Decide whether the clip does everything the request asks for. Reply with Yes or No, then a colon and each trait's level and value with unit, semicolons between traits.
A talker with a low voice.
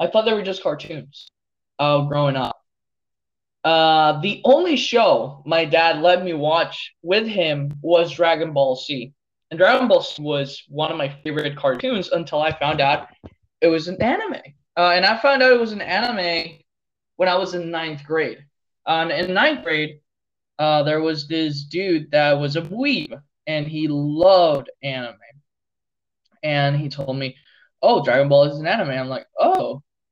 No: medium, 155 Hz